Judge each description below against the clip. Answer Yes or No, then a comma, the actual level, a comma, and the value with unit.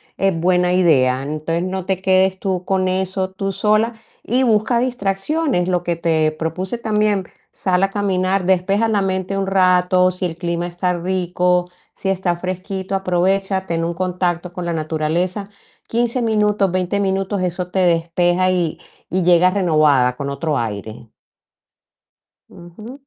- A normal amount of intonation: No, narrow, 2.0 semitones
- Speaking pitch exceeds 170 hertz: Yes, medium, 185 Hz